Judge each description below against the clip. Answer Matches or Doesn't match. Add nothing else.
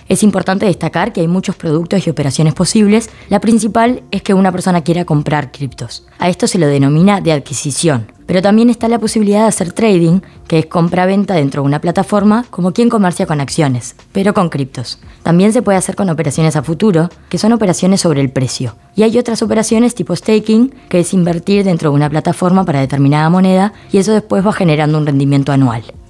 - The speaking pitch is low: Doesn't match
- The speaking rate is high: Matches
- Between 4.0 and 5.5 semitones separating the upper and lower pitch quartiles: Matches